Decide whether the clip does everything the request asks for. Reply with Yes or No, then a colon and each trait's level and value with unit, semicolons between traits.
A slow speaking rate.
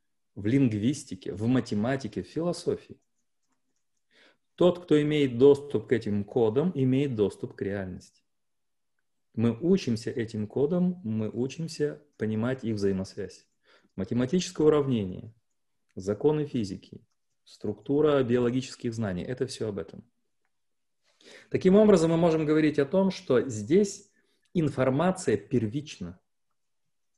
Yes: slow, 105 wpm